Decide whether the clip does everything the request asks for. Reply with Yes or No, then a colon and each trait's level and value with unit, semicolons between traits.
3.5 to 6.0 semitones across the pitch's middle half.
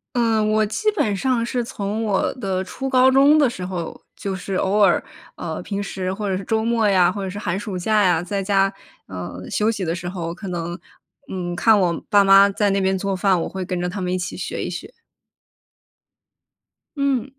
No: average, 3.1 semitones